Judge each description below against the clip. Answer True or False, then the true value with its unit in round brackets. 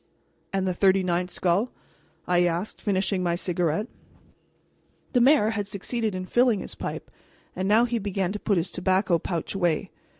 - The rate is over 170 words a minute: False (165 wpm)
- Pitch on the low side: False (190 Hz)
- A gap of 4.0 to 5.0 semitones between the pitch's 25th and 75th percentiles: False (2.9 semitones)